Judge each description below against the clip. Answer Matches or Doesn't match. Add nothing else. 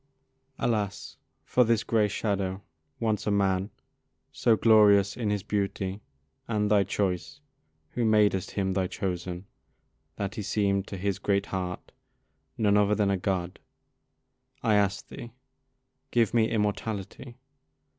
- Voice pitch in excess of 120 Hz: Doesn't match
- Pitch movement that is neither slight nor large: Doesn't match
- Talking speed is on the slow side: Matches